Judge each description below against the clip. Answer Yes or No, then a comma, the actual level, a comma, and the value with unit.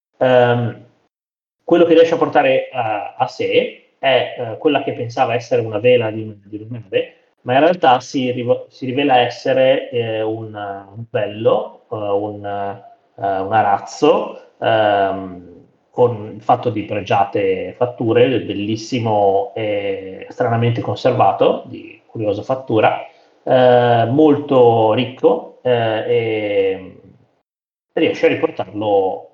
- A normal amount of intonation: No, wide, 6.5 semitones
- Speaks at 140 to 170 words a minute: No, average, 120 wpm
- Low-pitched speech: Yes, low, 120 Hz